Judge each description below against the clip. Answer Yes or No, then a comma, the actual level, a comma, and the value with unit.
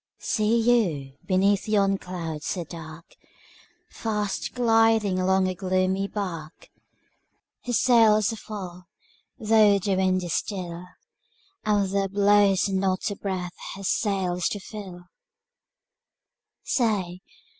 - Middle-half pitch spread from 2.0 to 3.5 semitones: Yes, narrow, 2.6 semitones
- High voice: Yes, high, 195 Hz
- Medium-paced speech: No, slow, 110 wpm